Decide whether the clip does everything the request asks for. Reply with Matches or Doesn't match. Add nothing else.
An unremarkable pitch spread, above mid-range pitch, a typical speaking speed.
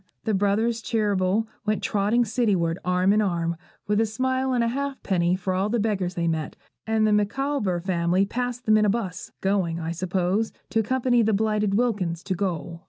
Matches